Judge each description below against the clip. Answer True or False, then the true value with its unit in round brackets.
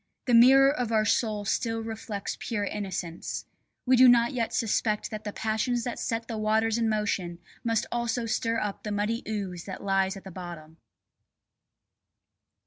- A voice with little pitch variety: True (2.3 semitones)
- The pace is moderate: True (165 wpm)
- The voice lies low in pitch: False (220 Hz)